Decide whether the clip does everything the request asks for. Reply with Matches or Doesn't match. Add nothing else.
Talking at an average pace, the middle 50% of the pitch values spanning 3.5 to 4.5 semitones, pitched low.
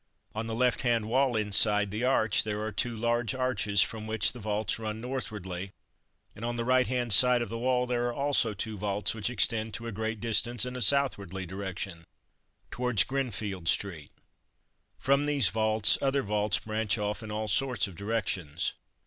Doesn't match